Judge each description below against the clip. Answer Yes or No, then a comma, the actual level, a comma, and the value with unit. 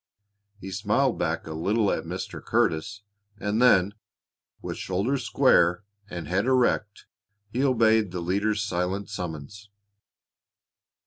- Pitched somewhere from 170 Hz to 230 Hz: No, low, 100 Hz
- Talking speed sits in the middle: No, slow, 120 wpm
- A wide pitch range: No, average, 3.3 semitones